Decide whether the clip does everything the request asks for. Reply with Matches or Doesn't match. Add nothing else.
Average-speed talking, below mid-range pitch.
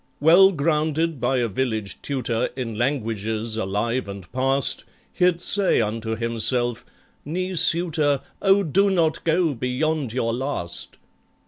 Doesn't match